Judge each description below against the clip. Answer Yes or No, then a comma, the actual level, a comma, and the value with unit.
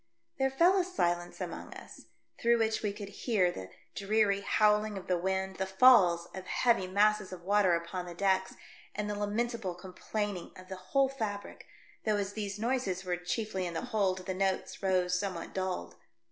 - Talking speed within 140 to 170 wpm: No, average, 185 wpm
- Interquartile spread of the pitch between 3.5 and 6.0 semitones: No, average, 2.7 semitones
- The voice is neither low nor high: No, high, 195 Hz